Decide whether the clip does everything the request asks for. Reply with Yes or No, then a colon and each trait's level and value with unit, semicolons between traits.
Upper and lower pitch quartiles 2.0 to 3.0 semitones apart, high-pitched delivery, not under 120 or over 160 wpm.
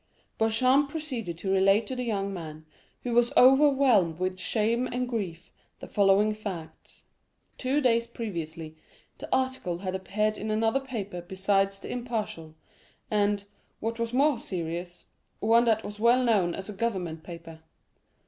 No: average, 4.4 semitones; high, 210 Hz; average, 150 wpm